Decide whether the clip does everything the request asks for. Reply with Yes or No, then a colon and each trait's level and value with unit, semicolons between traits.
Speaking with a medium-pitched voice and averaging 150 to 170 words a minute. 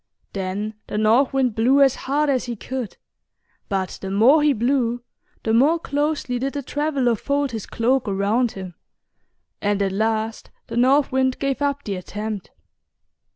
No: high, 245 Hz; average, 160 wpm